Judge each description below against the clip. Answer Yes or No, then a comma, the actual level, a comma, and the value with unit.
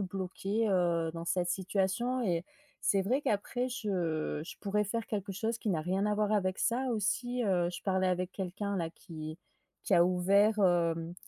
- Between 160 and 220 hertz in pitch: Yes, high, 190 Hz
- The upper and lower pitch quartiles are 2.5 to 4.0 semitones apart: Yes, average, 3.2 semitones